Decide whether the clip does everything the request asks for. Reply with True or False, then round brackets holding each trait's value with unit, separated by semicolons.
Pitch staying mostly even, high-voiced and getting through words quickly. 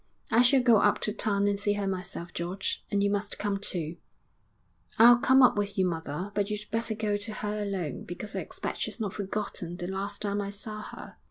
True (1.7 semitones; 205 Hz; 220 wpm)